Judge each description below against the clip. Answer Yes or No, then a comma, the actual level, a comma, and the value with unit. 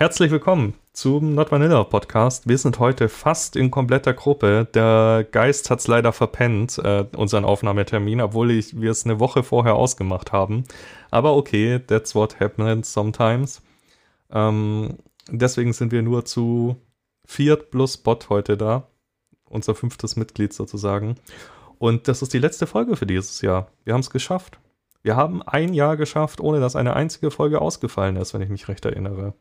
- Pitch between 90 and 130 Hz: Yes, low, 115 Hz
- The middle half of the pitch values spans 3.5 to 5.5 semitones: Yes, average, 3.8 semitones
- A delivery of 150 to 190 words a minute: Yes, average, 160 wpm